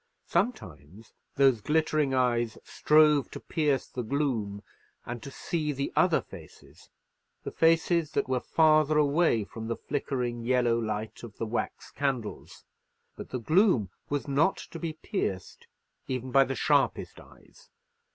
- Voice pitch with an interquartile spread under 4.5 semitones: No, average, 4.8 semitones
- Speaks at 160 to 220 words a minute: No, average, 140 wpm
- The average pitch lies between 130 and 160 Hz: Yes, low, 135 Hz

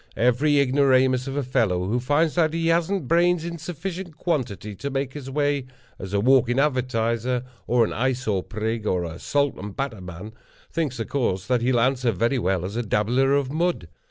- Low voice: Yes, low, 130 Hz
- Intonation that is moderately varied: Yes, average, 4.4 semitones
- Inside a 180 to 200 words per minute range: Yes, average, 195 wpm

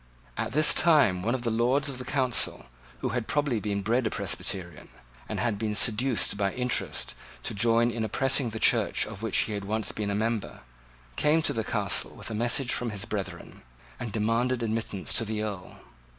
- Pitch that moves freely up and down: No, average, 2.8 semitones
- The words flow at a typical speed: Yes, average, 195 wpm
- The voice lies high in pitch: No, low, 115 Hz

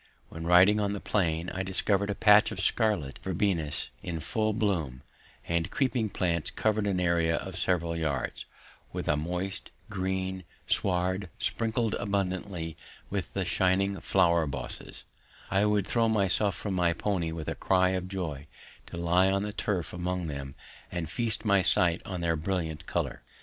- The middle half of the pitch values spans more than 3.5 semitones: No, average, 3.2 semitones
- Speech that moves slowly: No, average, 160 wpm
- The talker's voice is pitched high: No, very low, 95 Hz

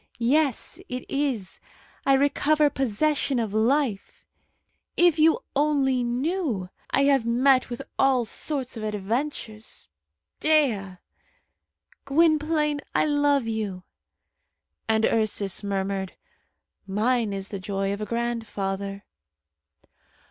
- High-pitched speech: Yes, high, 240 Hz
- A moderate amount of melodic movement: No, wide, 5.8 semitones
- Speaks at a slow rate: Yes, slow, 105 wpm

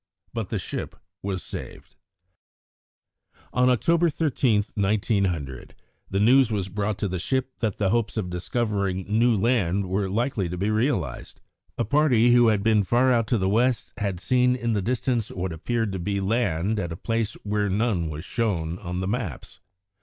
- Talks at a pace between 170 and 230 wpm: Yes, average, 175 wpm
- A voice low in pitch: Yes, low, 105 Hz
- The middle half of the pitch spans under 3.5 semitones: No, average, 4.0 semitones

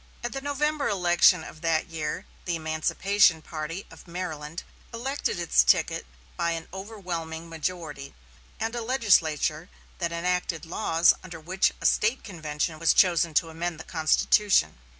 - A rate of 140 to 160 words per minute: Yes, average, 145 wpm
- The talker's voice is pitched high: No, medium, 170 Hz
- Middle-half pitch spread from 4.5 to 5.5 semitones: No, average, 3.3 semitones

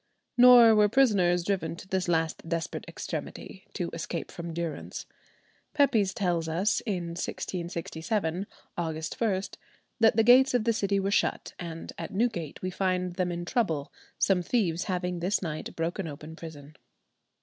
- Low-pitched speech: No, medium, 180 Hz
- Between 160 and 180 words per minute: No, average, 150 wpm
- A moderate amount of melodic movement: Yes, average, 3.6 semitones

